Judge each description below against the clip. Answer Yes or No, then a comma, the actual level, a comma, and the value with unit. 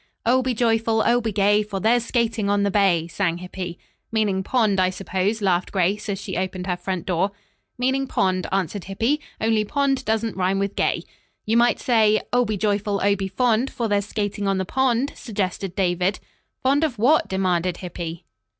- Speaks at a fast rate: No, average, 185 wpm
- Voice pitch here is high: Yes, high, 205 Hz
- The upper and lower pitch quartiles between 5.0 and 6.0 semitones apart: No, average, 3.4 semitones